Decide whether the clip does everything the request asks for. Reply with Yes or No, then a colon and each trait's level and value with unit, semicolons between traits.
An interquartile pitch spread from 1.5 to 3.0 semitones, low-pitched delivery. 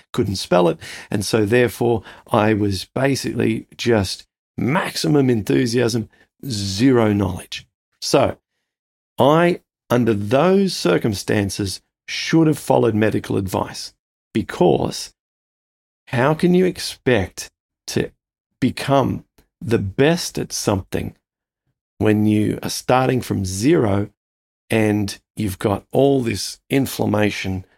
No: average, 4.6 semitones; low, 110 Hz